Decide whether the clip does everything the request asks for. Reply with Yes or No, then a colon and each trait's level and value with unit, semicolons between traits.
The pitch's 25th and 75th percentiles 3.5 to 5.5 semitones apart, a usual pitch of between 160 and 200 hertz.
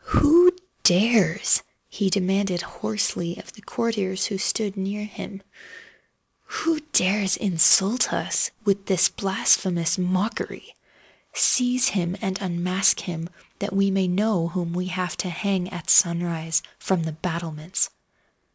No: narrow, 2.6 semitones; high, 190 Hz